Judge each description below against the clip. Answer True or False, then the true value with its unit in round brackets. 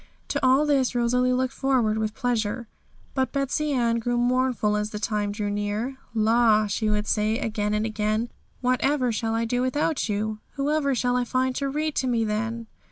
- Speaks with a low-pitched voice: False (235 Hz)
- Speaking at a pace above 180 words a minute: True (190 wpm)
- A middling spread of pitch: True (3.2 semitones)